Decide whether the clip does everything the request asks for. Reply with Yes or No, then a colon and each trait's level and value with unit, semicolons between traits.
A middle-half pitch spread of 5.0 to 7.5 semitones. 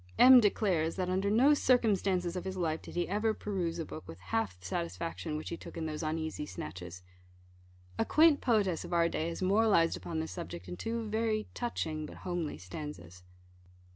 Yes: wide, 5.5 semitones